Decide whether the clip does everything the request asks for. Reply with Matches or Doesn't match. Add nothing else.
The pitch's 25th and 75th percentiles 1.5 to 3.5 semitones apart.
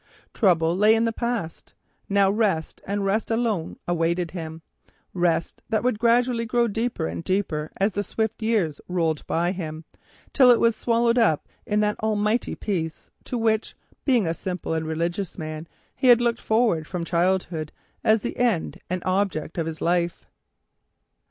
Doesn't match